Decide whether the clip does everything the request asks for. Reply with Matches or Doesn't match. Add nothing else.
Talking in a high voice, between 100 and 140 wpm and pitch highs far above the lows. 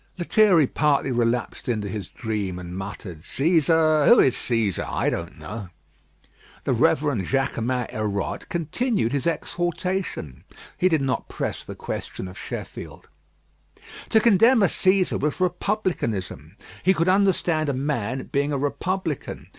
Doesn't match